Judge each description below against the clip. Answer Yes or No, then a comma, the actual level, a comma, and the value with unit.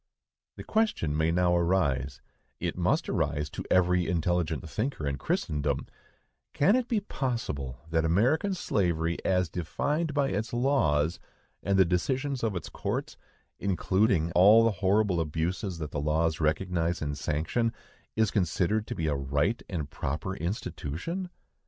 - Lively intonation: Yes, wide, 6.0 semitones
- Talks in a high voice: No, very low, 90 Hz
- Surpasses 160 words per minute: No, average, 140 wpm